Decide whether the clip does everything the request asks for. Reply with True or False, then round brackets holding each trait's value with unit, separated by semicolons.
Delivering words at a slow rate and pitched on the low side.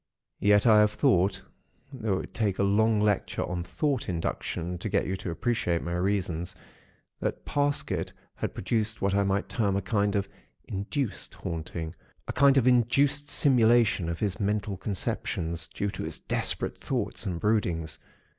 False (165 wpm; 100 Hz)